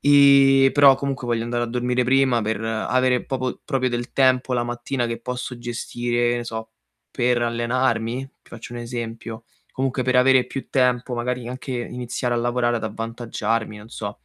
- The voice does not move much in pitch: Yes, narrow, 1.5 semitones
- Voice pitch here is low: Yes, low, 120 Hz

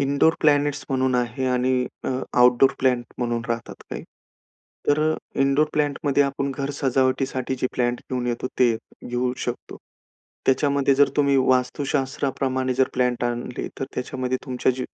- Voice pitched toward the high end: No, low, 130 Hz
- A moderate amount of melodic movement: No, narrow, 1.8 semitones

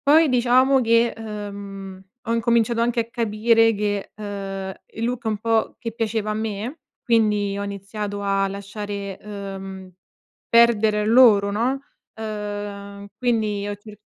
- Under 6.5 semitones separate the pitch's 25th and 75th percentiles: Yes, narrow, 2.4 semitones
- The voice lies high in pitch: Yes, high, 210 Hz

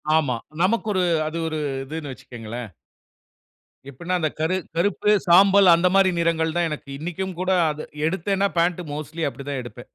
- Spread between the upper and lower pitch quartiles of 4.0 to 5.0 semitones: No, average, 3.6 semitones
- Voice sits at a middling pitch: Yes, medium, 165 Hz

